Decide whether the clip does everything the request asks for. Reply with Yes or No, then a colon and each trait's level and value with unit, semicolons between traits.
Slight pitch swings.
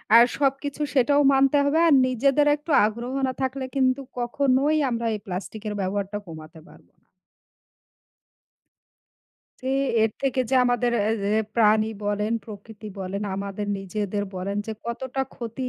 No: average, 4.4 semitones